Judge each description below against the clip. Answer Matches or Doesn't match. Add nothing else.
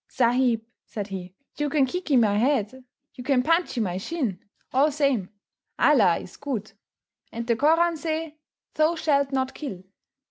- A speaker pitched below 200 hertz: Doesn't match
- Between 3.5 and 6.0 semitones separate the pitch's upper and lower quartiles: Matches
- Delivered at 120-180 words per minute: Matches